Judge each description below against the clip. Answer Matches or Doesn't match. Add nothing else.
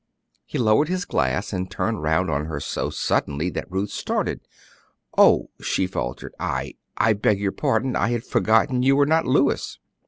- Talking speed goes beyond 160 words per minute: Matches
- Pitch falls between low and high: Doesn't match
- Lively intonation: Matches